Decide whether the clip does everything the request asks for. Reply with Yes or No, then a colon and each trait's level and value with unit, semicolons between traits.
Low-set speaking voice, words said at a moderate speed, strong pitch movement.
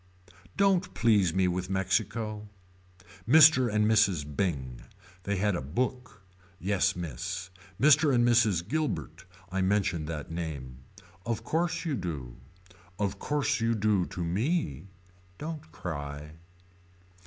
No: low, 100 Hz; slow, 120 wpm; wide, 5.8 semitones